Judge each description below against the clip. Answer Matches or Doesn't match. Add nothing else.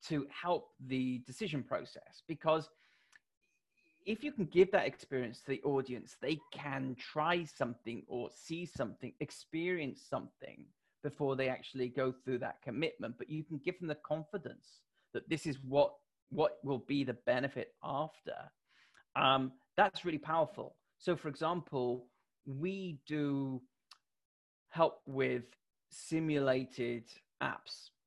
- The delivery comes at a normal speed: Doesn't match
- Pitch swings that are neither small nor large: Matches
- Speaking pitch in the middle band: Matches